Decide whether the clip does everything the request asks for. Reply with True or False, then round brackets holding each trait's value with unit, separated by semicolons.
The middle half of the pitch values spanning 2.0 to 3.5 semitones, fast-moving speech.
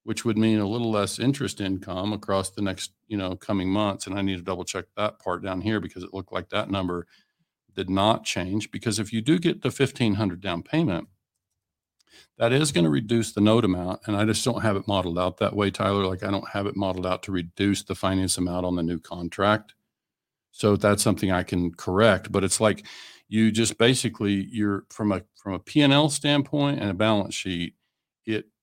True (2.7 semitones; 215 wpm)